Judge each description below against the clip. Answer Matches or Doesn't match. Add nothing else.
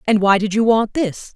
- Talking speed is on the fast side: Matches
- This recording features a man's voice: Doesn't match